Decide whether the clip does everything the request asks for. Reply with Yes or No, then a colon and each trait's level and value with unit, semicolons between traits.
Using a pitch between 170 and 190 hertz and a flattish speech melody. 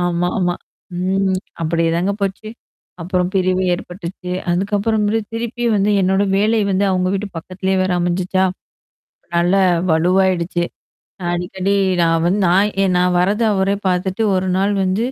Yes: medium, 185 Hz; narrow, 2.0 semitones